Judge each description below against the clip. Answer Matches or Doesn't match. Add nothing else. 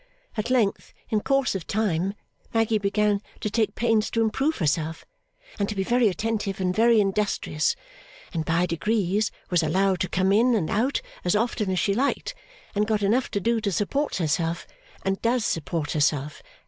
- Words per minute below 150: Doesn't match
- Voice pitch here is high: Matches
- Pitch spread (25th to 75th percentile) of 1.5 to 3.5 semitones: Doesn't match